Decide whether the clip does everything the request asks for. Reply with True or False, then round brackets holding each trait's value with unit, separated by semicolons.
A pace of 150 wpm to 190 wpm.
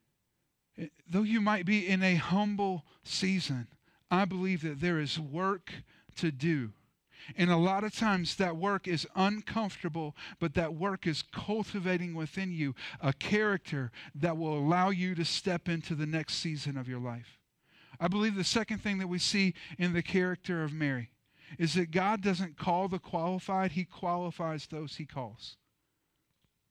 True (165 wpm)